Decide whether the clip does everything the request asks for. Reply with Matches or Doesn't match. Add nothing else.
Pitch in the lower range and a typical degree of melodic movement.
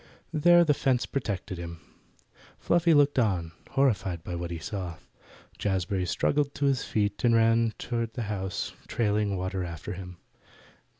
Doesn't match